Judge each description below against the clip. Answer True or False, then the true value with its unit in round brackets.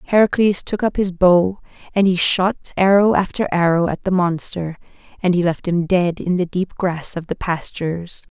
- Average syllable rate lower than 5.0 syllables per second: True (4.7 syllables/s)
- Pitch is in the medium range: True (180 Hz)